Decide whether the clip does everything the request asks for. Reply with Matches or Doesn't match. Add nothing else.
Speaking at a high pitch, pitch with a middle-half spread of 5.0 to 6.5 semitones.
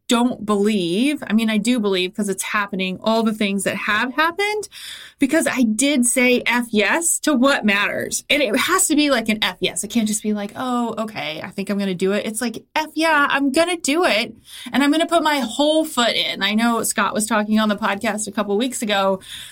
Matches